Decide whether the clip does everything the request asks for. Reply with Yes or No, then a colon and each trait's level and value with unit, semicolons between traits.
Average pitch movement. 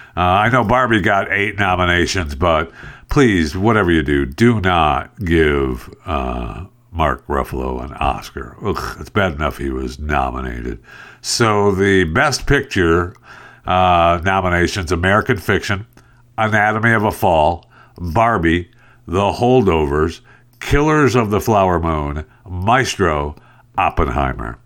No: wide, 6.0 semitones